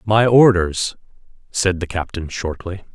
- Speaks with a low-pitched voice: Yes, very low, 95 Hz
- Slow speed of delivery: Yes, slow, 120 wpm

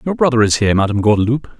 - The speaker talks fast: Yes, fast, 225 wpm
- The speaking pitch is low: Yes, low, 120 Hz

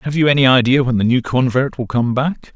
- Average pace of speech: No, fast, 260 wpm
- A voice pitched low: Yes, low, 130 Hz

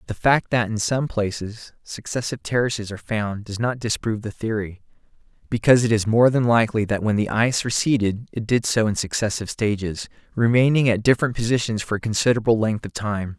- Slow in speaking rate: No, average, 190 wpm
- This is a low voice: Yes, low, 110 Hz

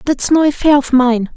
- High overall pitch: Yes, very high, 270 Hz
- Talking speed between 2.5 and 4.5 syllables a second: No, 5.0 syllables/s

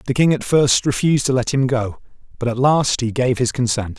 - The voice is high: No, low, 130 Hz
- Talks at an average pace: No, fast, 240 wpm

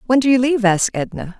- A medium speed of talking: No, fast, 260 wpm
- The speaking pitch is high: Yes, high, 230 Hz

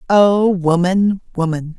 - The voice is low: No, medium, 185 Hz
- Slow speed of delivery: Yes, slow, 100 wpm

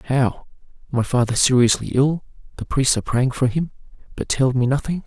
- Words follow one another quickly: No, average, 180 wpm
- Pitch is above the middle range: No, low, 130 Hz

